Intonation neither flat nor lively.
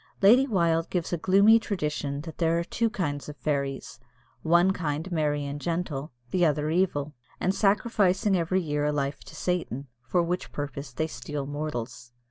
Yes: average, 3.9 semitones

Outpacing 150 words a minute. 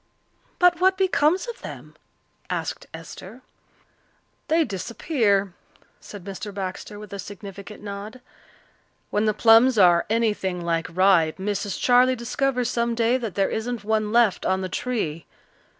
No: slow, 135 wpm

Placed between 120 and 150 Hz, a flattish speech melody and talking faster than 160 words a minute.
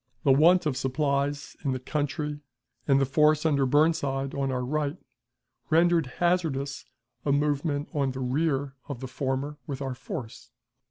No: medium, 140 Hz; narrow, 2.2 semitones; average, 155 wpm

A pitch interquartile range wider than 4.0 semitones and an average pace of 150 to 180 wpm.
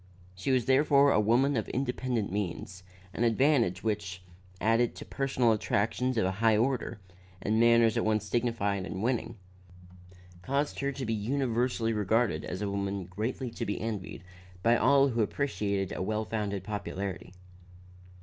No: average, 3.7 semitones; average, 155 wpm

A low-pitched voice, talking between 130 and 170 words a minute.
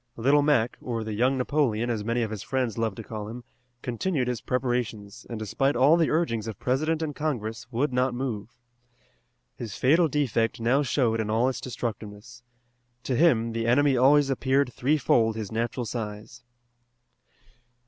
Yes: low, 120 Hz; average, 165 wpm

